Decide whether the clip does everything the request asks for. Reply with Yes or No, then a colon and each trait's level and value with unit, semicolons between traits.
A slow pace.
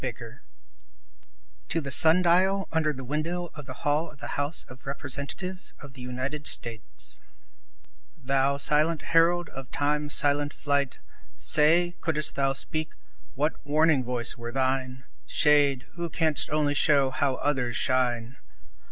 No: average, 145 wpm